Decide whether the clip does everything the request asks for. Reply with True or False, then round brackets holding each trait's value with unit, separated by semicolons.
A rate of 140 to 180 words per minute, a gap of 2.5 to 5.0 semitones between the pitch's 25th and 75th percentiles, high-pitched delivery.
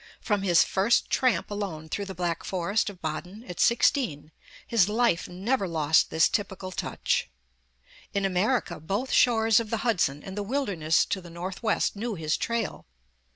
True (165 wpm; 4.7 semitones; 195 Hz)